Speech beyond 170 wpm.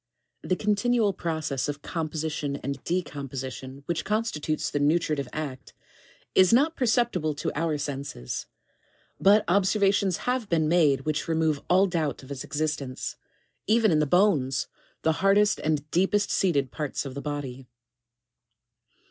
No: average, 140 wpm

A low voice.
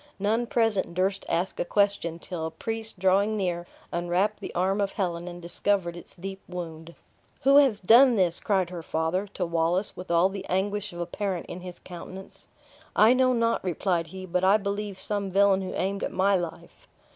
No: high, 190 Hz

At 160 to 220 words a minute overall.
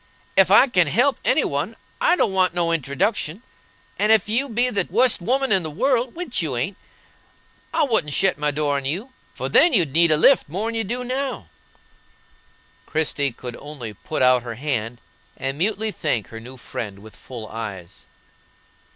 Yes: average, 180 wpm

